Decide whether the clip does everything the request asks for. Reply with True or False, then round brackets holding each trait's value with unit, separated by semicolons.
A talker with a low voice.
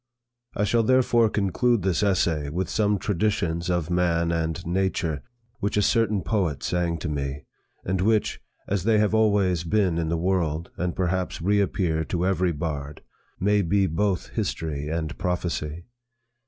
True (90 Hz)